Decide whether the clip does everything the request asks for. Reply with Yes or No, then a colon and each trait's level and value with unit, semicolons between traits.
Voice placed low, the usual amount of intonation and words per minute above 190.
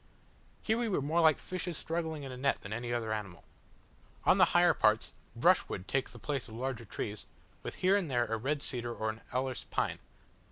No: low, 130 Hz; wide, 5.8 semitones; fast, 205 wpm